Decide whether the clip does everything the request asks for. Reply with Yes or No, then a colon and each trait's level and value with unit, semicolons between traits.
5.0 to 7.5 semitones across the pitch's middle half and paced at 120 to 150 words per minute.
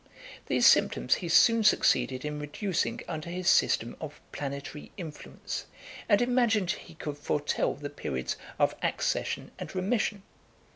Yes: wide, 5.4 semitones; slow, 135 wpm